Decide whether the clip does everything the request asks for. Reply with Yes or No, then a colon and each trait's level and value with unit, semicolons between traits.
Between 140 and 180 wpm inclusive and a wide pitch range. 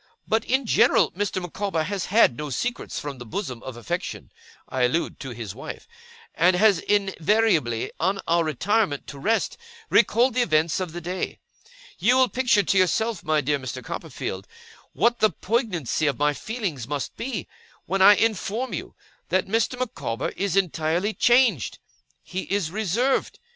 Yes: average, 160 wpm; wide, 6.6 semitones